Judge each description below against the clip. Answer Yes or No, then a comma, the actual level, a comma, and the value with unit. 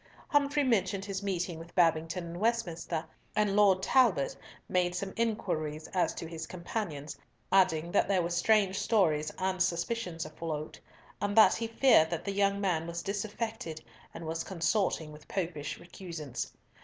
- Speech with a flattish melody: No, average, 3.8 semitones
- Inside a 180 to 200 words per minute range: No, average, 155 wpm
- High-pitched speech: No, medium, 180 Hz